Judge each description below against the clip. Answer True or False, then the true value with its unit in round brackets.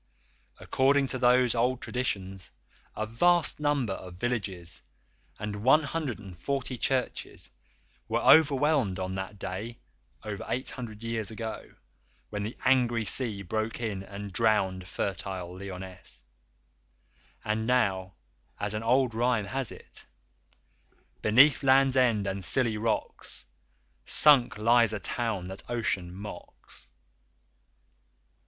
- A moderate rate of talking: False (115 wpm)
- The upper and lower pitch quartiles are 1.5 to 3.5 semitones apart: False (4.4 semitones)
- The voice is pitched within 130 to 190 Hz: False (110 Hz)